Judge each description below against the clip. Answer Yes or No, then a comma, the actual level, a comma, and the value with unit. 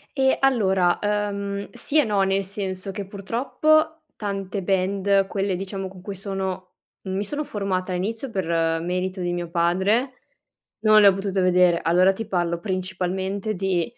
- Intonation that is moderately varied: No, narrow, 1.9 semitones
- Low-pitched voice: No, high, 195 Hz